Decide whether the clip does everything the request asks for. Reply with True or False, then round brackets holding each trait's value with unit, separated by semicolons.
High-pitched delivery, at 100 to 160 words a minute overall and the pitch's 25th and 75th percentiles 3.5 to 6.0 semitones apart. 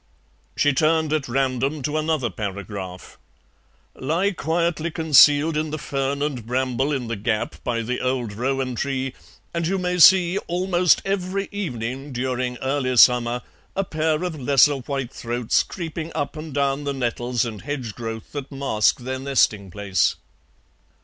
False (135 Hz; 150 wpm; 4.3 semitones)